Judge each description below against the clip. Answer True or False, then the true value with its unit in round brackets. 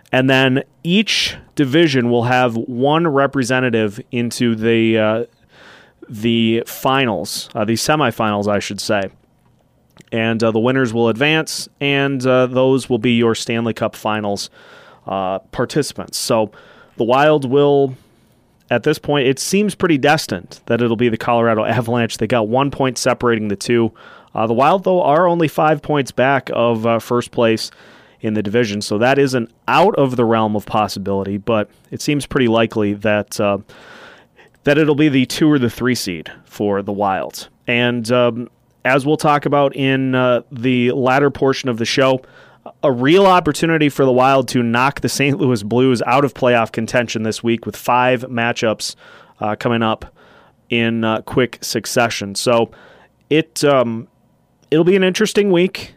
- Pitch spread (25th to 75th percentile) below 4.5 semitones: True (3.5 semitones)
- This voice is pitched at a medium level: False (125 Hz)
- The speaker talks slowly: False (165 wpm)